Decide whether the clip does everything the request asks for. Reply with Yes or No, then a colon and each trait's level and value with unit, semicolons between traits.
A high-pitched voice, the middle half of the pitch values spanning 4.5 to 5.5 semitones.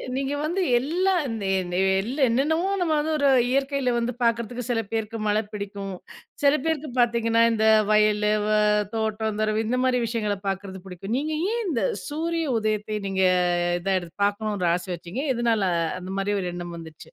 Yes: high, 225 Hz; average, 5.1 semitones